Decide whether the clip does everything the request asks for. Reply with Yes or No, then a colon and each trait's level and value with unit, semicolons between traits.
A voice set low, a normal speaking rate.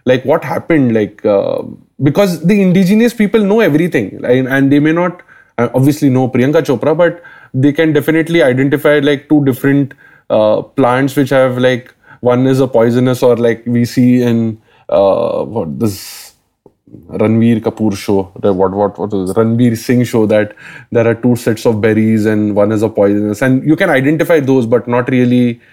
Yes: low, 125 Hz; average, 180 wpm